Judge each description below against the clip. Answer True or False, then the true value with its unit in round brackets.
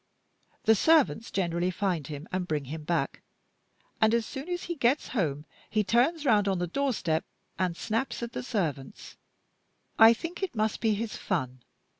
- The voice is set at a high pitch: True (210 Hz)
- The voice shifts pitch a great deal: True (5.9 semitones)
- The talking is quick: False (170 wpm)